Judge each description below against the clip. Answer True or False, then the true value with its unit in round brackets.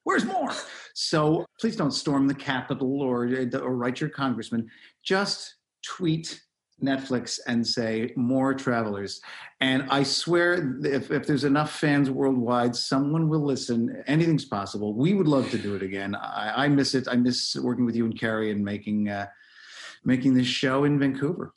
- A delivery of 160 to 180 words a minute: True (165 wpm)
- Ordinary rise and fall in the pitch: True (3.4 semitones)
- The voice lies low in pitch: True (130 Hz)